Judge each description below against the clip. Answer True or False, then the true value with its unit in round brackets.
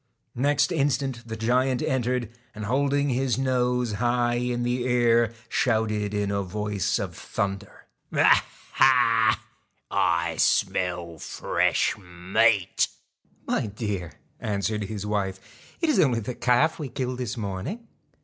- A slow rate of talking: True (130 wpm)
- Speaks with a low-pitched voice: True (115 Hz)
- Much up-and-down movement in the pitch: False (3.7 semitones)